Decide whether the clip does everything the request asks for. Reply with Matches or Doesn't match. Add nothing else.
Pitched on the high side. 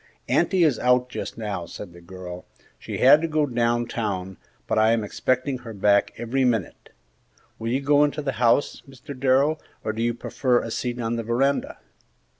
Doesn't match